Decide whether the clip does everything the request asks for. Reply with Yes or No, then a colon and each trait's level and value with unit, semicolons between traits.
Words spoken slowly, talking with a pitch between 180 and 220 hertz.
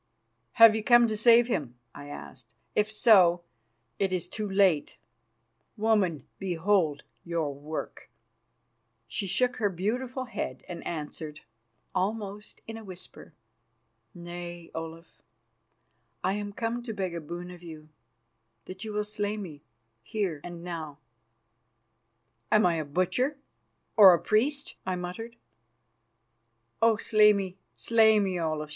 Yes: slow, 130 wpm; high, 190 Hz